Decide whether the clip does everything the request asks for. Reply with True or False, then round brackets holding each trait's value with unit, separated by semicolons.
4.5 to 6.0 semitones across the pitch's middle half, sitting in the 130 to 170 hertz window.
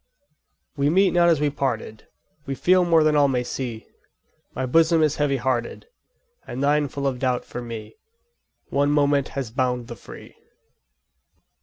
False (3.3 semitones; 140 Hz)